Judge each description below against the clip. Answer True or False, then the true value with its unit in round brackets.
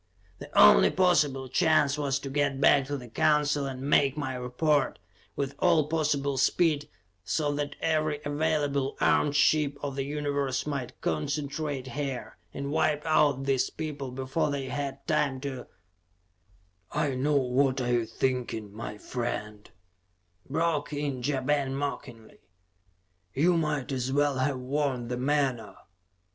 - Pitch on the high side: False (140 Hz)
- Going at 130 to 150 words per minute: True (140 wpm)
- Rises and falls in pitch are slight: True (2.1 semitones)